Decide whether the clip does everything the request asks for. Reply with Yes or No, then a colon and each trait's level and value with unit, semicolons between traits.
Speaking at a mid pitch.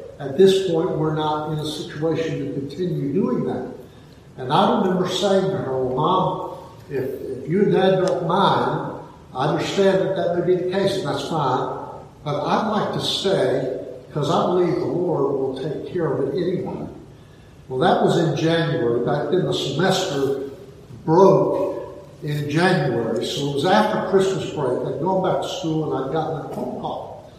Yes: medium, 180 Hz